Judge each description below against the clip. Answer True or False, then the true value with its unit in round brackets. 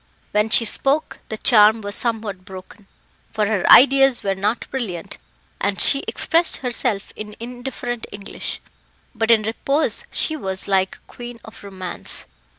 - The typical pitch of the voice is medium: False (220 Hz)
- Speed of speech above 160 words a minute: False (150 wpm)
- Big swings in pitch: False (3.4 semitones)